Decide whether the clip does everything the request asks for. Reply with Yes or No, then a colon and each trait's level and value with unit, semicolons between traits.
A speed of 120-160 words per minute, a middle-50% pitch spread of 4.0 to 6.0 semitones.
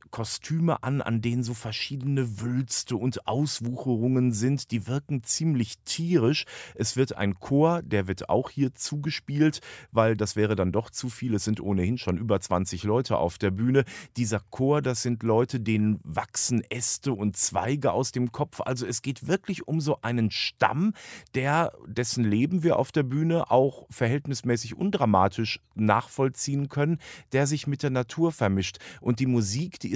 No: average, 170 wpm; average, 4.3 semitones